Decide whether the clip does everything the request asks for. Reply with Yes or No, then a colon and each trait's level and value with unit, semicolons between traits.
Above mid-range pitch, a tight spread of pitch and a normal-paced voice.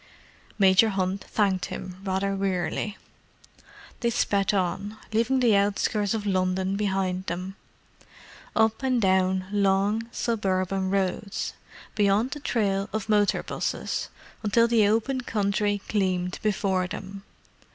No: high, 200 Hz; narrow, 2.3 semitones; slow, 120 wpm